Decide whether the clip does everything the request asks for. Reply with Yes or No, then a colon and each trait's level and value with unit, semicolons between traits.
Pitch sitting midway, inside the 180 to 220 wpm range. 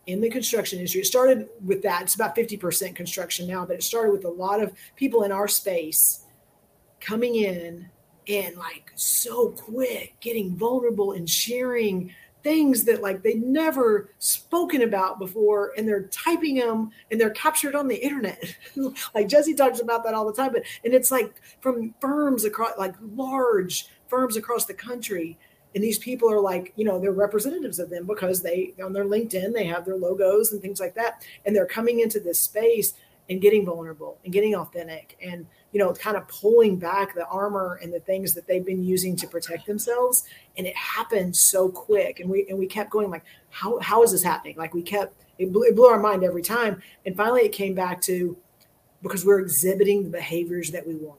No: high, 205 Hz; average, 200 wpm